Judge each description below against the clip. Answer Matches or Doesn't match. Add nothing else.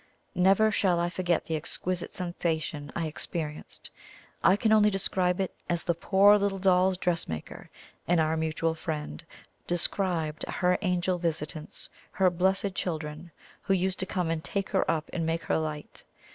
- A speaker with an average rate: Matches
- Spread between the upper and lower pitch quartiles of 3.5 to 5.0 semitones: Doesn't match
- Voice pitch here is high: Doesn't match